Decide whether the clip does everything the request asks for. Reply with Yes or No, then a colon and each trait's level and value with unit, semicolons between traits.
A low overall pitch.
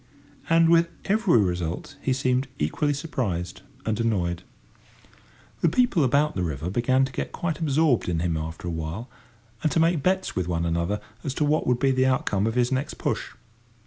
Yes: low, 125 Hz